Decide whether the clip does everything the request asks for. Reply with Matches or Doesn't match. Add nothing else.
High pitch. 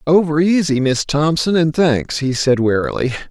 Doesn't match